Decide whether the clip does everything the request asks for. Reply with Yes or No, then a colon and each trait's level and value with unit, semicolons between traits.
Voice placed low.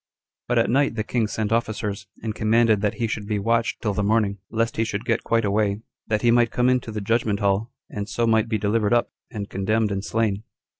Yes: low, 110 Hz